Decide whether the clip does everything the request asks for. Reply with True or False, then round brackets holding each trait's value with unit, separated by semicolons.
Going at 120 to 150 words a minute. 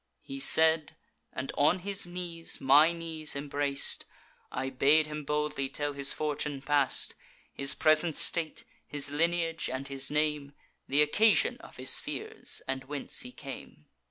True (145 wpm)